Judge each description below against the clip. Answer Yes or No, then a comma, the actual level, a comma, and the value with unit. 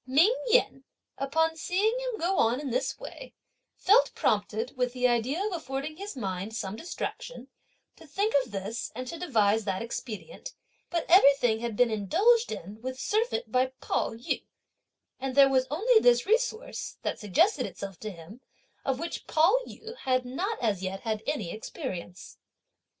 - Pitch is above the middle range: Yes, very high, 265 Hz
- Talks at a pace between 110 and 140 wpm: No, average, 165 wpm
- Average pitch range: No, wide, 8.9 semitones